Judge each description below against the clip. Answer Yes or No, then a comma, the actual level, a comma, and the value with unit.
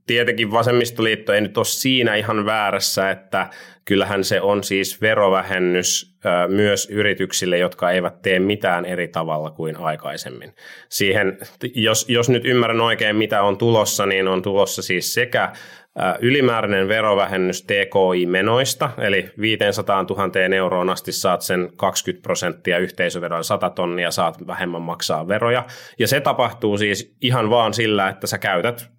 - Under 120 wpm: No, average, 140 wpm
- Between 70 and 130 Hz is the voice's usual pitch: Yes, low, 100 Hz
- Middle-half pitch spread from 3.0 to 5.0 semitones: Yes, average, 3.3 semitones